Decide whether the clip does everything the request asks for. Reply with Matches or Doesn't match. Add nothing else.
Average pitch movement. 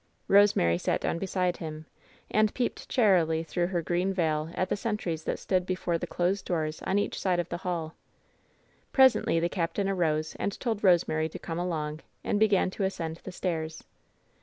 Matches